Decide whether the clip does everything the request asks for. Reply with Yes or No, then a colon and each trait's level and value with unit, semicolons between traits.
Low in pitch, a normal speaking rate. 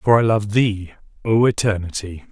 Yes: low, 105 Hz; average, 155 wpm